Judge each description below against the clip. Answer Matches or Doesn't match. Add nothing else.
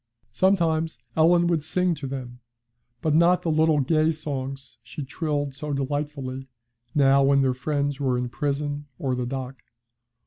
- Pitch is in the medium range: Matches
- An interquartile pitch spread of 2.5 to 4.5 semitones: Matches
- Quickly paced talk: Doesn't match